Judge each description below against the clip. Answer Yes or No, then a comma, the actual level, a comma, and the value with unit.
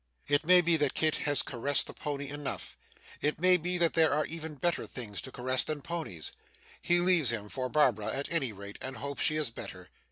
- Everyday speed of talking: No, fast, 215 wpm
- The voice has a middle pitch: Yes, medium, 145 Hz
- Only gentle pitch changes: No, average, 4.0 semitones